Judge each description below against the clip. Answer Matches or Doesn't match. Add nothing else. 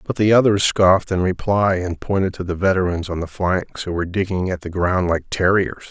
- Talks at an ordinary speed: Doesn't match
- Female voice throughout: Doesn't match